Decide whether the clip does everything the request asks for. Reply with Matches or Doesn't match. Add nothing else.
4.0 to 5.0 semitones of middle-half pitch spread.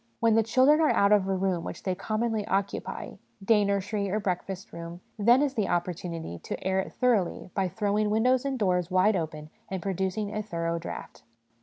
Doesn't match